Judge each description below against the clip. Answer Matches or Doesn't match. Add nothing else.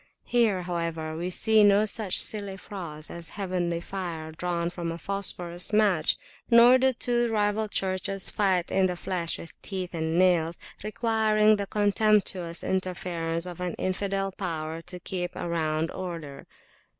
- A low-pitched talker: Doesn't match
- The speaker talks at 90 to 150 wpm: Matches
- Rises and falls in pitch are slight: Doesn't match